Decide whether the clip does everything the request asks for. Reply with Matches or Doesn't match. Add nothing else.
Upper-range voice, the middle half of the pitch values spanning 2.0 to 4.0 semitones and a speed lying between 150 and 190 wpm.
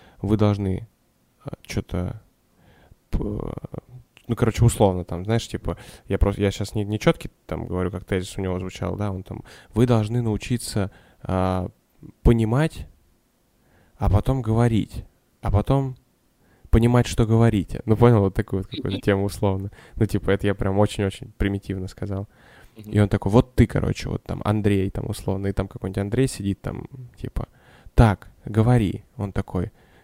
Doesn't match